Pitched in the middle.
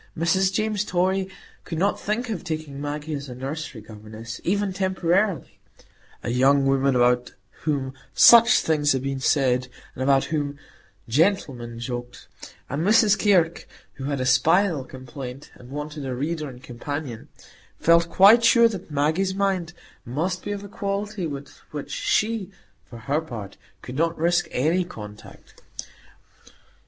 Yes: medium, 150 Hz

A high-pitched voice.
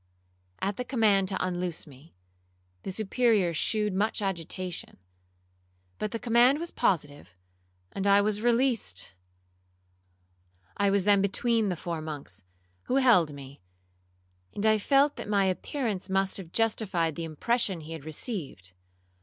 Yes: high, 195 Hz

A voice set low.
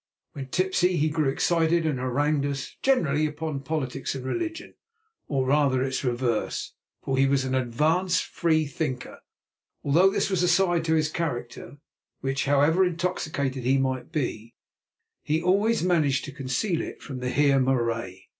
No: medium, 145 Hz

